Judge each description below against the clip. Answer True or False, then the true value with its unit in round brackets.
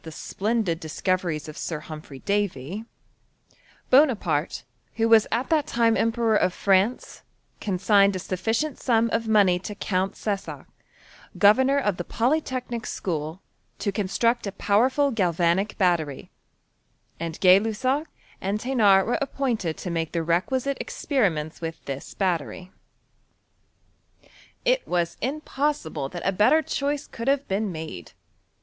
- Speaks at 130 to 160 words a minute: True (135 wpm)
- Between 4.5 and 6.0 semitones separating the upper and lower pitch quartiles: True (5.6 semitones)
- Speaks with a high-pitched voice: True (200 Hz)